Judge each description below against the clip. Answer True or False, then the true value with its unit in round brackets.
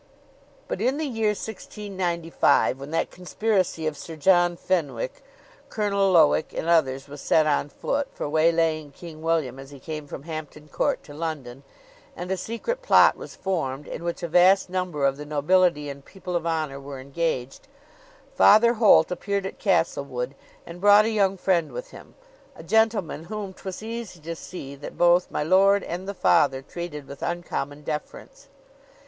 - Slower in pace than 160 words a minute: False (170 wpm)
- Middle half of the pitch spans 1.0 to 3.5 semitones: False (4.5 semitones)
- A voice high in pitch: False (170 Hz)